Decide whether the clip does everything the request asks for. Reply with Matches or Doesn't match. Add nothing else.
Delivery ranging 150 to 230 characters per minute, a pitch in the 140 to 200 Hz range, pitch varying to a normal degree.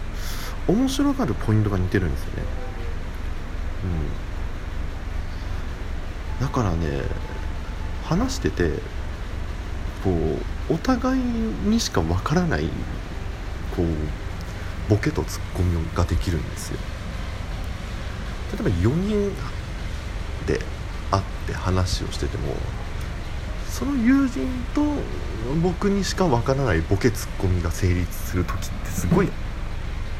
Doesn't match